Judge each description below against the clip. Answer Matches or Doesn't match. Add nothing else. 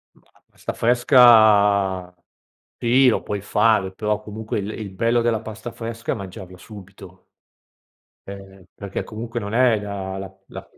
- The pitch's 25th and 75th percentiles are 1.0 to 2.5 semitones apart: Doesn't match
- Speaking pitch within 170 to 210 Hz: Doesn't match